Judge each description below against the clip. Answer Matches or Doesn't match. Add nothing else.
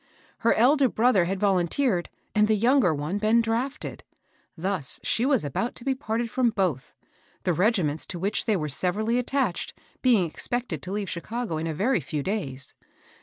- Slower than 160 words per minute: Doesn't match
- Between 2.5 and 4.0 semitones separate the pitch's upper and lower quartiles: Doesn't match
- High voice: Matches